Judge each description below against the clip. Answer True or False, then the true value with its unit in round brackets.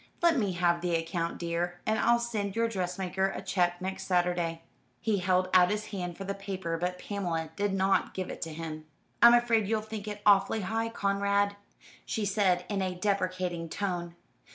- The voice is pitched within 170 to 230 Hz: True (190 Hz)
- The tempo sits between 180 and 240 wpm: True (185 wpm)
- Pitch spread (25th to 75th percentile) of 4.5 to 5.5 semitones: False (2.7 semitones)